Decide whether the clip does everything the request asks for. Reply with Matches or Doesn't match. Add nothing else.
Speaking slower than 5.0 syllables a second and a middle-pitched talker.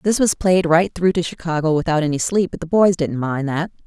Doesn't match